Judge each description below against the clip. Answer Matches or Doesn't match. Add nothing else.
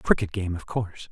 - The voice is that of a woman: Doesn't match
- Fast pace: Matches